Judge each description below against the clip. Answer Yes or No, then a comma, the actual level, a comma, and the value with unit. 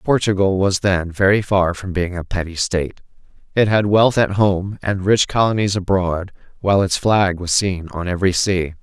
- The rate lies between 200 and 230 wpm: No, average, 185 wpm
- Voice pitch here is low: Yes, very low, 95 Hz